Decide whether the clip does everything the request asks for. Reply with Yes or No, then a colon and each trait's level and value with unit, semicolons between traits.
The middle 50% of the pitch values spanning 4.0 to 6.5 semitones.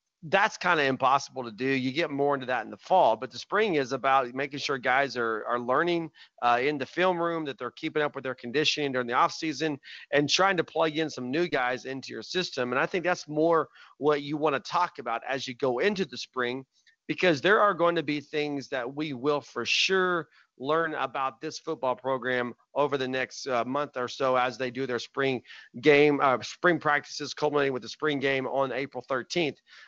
No: average, 3.3 semitones